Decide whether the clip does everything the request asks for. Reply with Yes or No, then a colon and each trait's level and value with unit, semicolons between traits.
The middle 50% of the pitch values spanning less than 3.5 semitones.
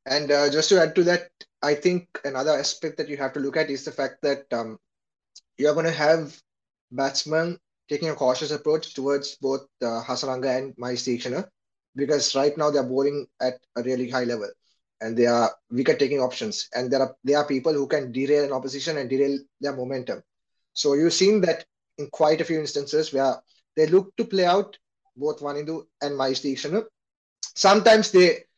Yes: average, 3.1 semitones